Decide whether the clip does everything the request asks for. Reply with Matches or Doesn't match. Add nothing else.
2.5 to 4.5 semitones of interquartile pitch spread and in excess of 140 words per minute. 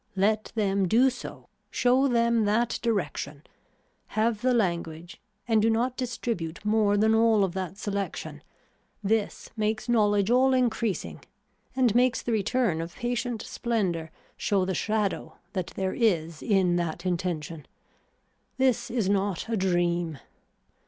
Doesn't match